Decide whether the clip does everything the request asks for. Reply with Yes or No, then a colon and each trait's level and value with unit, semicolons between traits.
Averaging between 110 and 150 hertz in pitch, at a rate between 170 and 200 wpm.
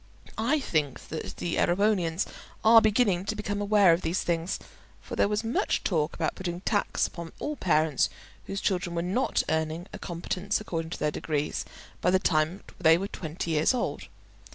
No: medium, 175 Hz; average, 180 wpm